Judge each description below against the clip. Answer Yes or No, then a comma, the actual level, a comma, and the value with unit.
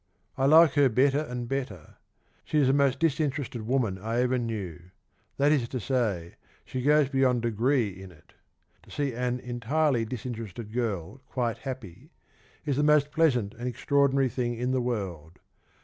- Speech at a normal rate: Yes, average, 165 wpm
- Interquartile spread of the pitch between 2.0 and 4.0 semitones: Yes, average, 3.5 semitones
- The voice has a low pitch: Yes, low, 125 Hz